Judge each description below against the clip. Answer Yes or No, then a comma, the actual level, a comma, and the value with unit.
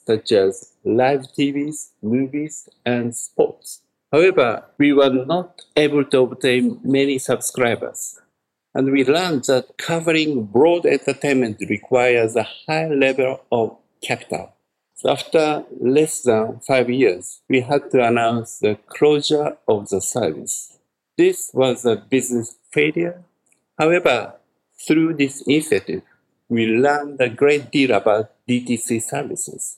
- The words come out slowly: Yes, slow, 125 wpm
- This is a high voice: No, low, 135 Hz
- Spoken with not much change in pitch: No, average, 3.8 semitones